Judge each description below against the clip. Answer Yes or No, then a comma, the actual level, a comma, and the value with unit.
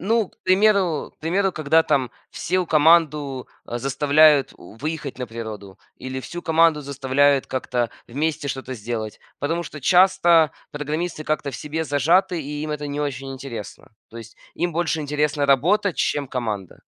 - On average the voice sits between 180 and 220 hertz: No, medium, 145 Hz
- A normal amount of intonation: Yes, average, 3.7 semitones